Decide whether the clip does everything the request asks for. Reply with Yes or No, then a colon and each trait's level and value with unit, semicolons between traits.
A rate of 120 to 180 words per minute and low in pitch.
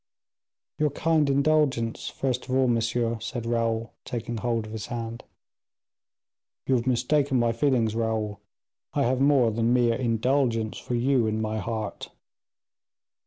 Yes: average, 140 wpm; low, 120 Hz